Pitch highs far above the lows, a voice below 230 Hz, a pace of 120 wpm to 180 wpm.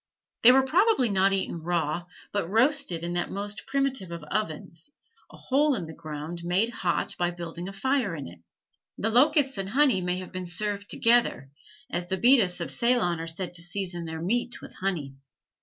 No: wide, 5.8 semitones; high, 190 Hz; average, 190 wpm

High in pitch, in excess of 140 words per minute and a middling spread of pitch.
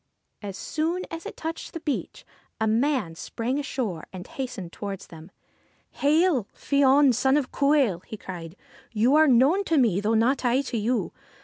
No: very high, 255 Hz; average, 185 wpm; wide, 5.9 semitones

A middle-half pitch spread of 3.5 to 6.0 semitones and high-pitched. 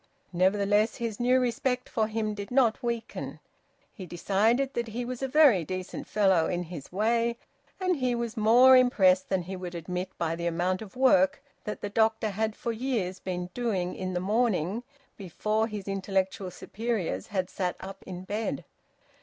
Yes: average, 4.2 semitones; high, 210 Hz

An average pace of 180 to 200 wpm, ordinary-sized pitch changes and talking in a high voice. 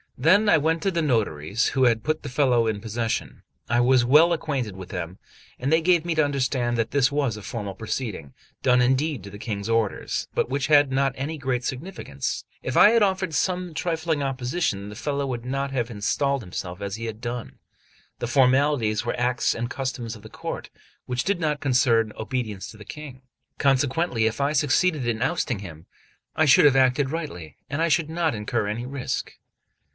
No: average, 195 wpm; average, 4.7 semitones; low, 130 Hz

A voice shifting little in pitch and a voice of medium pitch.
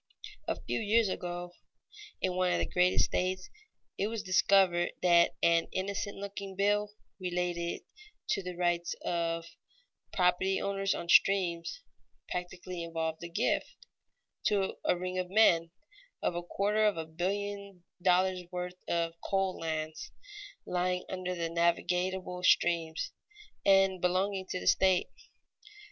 Yes: narrow, 1.9 semitones; medium, 180 Hz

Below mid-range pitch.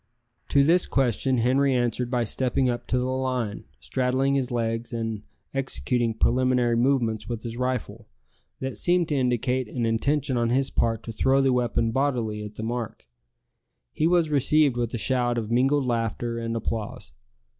Yes: low, 125 Hz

